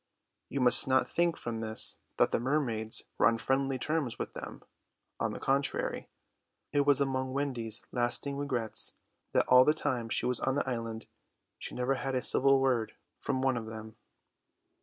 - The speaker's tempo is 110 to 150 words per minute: No, average, 175 wpm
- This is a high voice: No, low, 130 Hz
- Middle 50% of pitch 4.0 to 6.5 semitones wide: No, average, 2.9 semitones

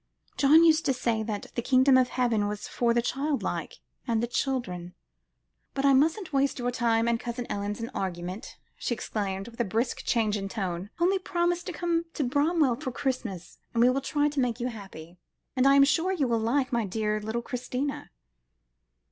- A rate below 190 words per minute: No, average, 200 wpm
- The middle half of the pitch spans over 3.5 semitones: Yes, average, 4.2 semitones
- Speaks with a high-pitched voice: Yes, high, 245 Hz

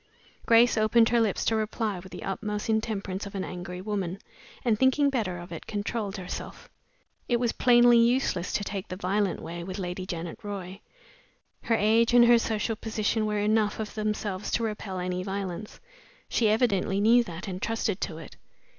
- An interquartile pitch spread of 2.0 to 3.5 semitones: Yes, average, 3.2 semitones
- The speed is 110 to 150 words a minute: No, average, 180 wpm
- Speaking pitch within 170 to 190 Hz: No, high, 210 Hz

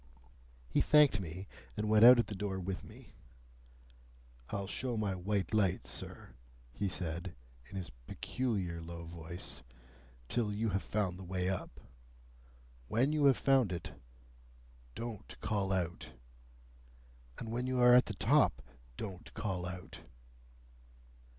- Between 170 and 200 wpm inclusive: No, slow, 135 wpm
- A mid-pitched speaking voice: No, very low, 95 Hz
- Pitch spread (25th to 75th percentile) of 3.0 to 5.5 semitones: Yes, average, 4.1 semitones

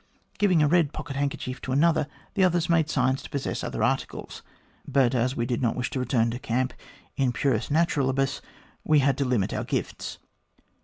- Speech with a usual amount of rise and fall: Yes, average, 3.4 semitones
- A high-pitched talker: No, low, 135 Hz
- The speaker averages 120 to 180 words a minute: No, average, 190 wpm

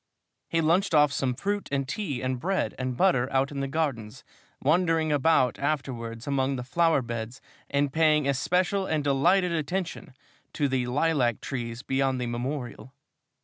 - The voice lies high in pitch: No, medium, 140 Hz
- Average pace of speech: Yes, average, 155 wpm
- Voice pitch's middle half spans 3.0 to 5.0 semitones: Yes, average, 4.1 semitones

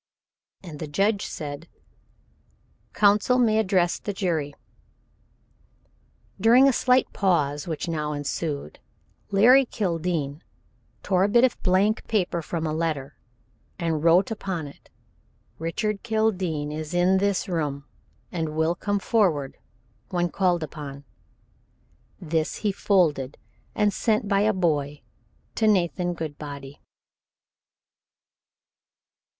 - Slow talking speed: Yes, slow, 110 wpm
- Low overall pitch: No, medium, 175 Hz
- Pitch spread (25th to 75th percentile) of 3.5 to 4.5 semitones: No, average, 4.9 semitones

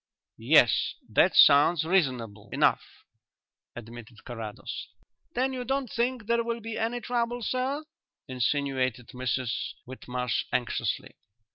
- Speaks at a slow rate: Yes, slow, 110 wpm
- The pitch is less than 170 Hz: Yes, medium, 140 Hz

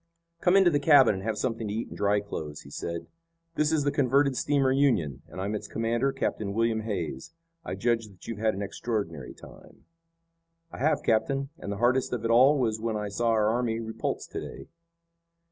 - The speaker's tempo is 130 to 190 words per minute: No, fast, 205 wpm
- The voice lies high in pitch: No, low, 115 Hz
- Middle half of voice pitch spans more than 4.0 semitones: Yes, average, 4.7 semitones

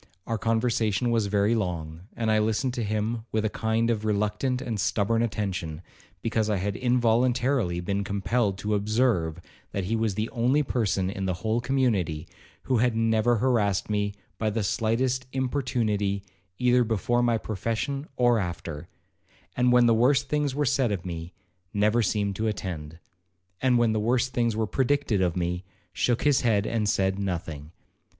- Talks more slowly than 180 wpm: Yes, average, 170 wpm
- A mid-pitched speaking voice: No, low, 110 Hz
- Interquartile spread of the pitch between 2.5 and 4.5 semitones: Yes, average, 3.4 semitones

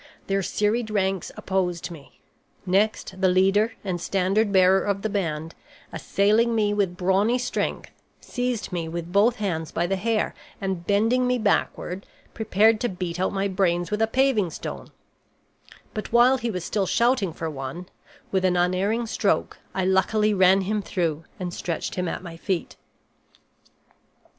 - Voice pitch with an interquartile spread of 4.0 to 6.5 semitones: No, average, 3.1 semitones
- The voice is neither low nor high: No, high, 195 Hz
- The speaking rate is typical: Yes, average, 155 wpm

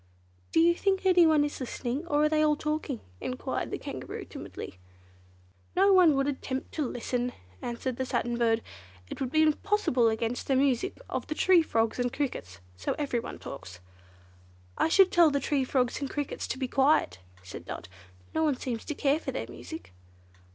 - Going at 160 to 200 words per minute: Yes, average, 180 wpm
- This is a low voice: No, very high, 275 Hz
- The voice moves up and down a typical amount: Yes, average, 4.4 semitones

